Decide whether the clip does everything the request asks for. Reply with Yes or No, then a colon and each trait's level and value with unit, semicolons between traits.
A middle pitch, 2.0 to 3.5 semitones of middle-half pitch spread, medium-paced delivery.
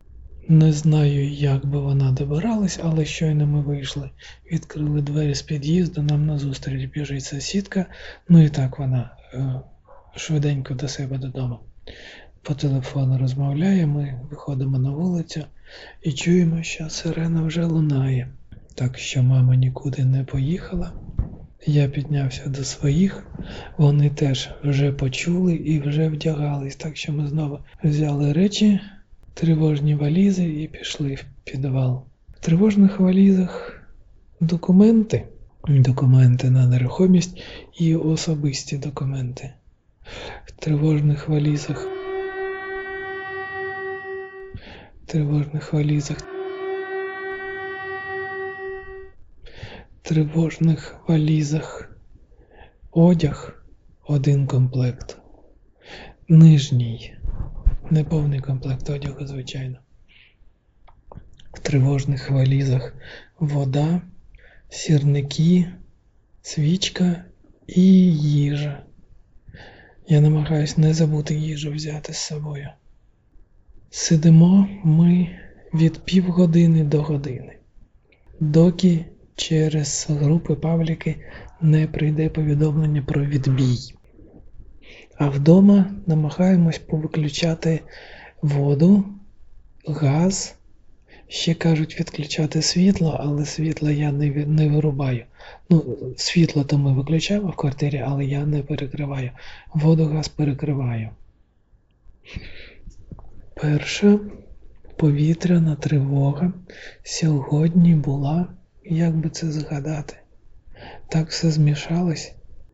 No: medium, 150 Hz; average, 3.1 semitones; slow, 90 wpm